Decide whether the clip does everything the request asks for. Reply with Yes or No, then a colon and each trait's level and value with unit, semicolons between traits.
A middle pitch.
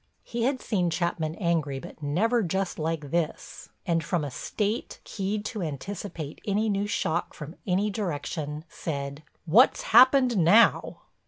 Yes: medium, 175 Hz